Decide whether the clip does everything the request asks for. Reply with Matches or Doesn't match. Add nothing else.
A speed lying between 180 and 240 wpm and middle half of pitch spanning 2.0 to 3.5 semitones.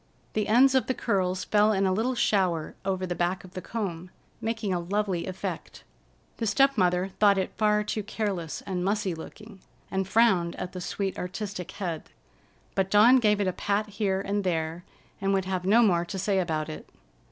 Matches